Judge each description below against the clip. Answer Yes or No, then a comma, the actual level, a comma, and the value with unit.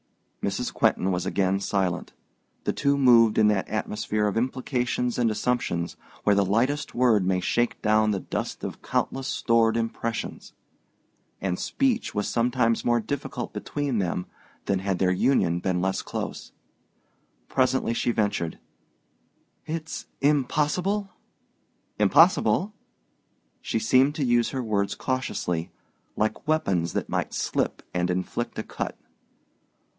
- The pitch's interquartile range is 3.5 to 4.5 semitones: No, average, 5.1 semitones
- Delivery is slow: Yes, slow, 130 wpm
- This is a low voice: Yes, low, 115 Hz